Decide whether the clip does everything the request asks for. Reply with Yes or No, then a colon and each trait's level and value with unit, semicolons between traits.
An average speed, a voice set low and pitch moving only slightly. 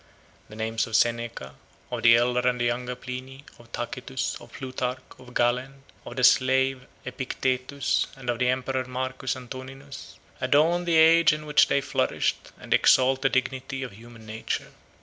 Yes: average, 165 wpm; low, 130 Hz; narrow, 1.7 semitones